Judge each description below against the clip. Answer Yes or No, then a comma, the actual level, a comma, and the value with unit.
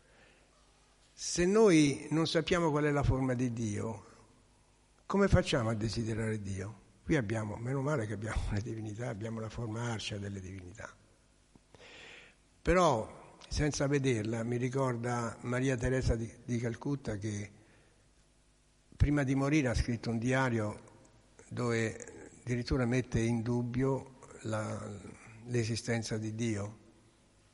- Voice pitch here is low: Yes, low, 115 Hz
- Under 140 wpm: Yes, average, 120 wpm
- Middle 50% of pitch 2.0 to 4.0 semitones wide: Yes, average, 2.9 semitones